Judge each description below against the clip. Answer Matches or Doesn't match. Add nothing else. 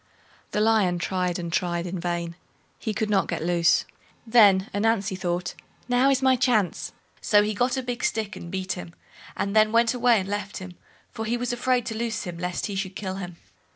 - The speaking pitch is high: Matches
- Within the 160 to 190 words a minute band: Doesn't match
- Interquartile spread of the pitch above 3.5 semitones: Matches